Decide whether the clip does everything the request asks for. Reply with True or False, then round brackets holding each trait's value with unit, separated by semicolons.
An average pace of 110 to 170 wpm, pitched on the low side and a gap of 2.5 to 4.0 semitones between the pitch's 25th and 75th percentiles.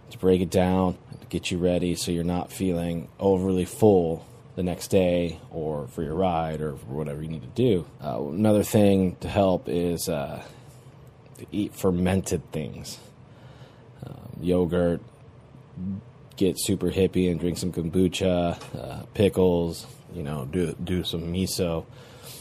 False (150 wpm; 90 Hz; 4.7 semitones)